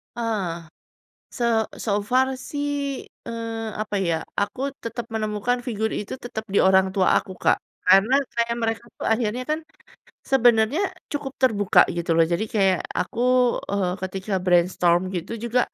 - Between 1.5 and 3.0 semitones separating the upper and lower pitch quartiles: No, average, 3.8 semitones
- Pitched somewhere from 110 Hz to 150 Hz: No, high, 215 Hz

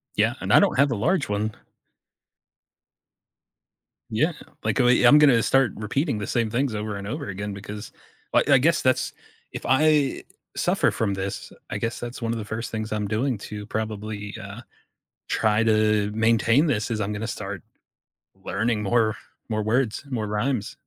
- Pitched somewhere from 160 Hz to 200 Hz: No, low, 110 Hz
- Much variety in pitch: No, average, 3.1 semitones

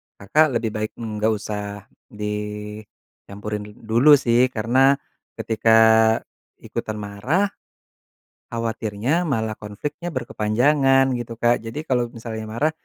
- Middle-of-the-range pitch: No, low, 115 Hz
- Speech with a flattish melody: No, average, 3.5 semitones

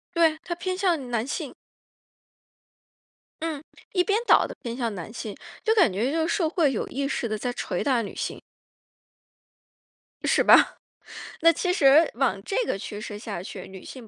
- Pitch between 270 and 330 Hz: Yes, very high, 275 Hz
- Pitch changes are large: Yes, wide, 7.0 semitones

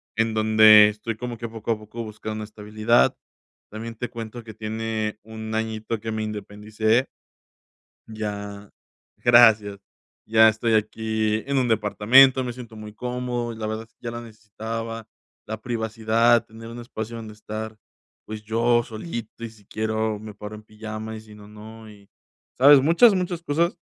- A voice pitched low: Yes, low, 110 Hz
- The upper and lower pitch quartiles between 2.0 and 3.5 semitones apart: No, narrow, 1.4 semitones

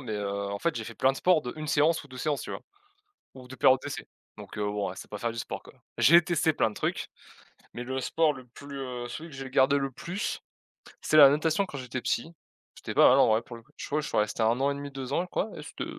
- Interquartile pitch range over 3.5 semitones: Yes, average, 3.9 semitones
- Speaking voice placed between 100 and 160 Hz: Yes, low, 135 Hz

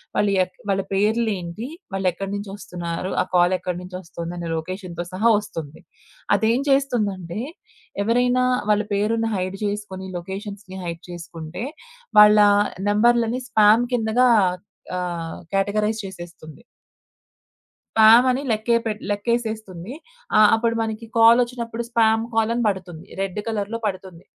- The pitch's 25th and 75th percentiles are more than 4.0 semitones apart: No, average, 3.7 semitones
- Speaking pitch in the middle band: No, high, 205 Hz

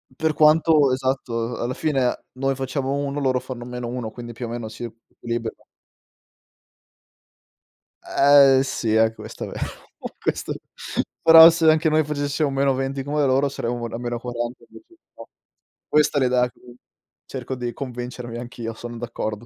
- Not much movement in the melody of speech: No, average, 3.0 semitones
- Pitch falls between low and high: No, low, 130 Hz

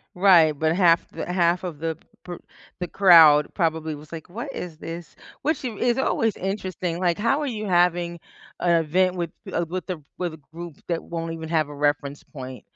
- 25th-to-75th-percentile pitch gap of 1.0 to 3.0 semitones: Yes, narrow, 2.4 semitones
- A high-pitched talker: No, medium, 170 Hz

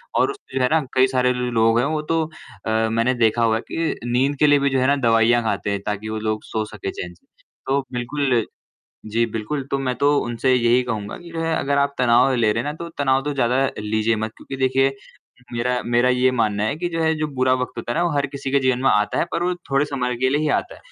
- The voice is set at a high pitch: No, low, 125 Hz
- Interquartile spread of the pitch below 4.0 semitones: Yes, average, 3.6 semitones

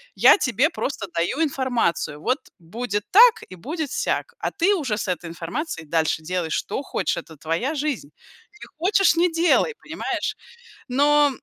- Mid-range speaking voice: No, very high, 255 Hz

